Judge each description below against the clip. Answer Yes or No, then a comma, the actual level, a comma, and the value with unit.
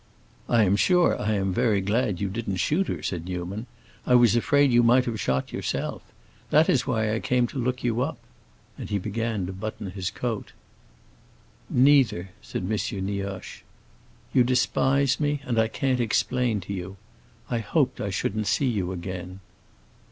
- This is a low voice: Yes, low, 110 Hz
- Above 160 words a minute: Yes, average, 170 wpm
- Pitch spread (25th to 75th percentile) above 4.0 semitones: Yes, average, 4.4 semitones